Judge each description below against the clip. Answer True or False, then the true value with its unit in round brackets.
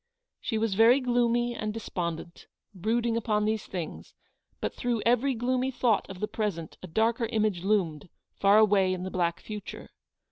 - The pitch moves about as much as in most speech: True (3.8 semitones)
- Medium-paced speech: True (165 wpm)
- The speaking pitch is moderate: False (215 Hz)